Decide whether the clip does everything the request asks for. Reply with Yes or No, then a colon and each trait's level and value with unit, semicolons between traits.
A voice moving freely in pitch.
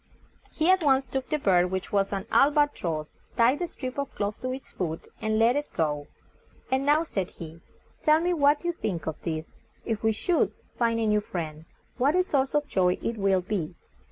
Yes: wide, 7.9 semitones